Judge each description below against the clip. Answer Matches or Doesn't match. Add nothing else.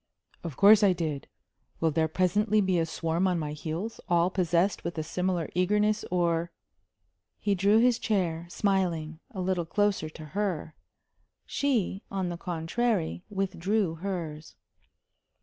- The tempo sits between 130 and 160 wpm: Matches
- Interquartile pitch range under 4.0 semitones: Matches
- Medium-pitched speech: Matches